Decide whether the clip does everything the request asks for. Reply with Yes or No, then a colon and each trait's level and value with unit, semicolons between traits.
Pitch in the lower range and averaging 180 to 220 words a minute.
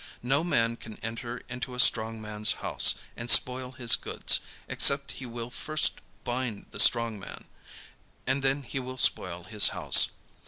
No: low, 120 Hz; average, 160 wpm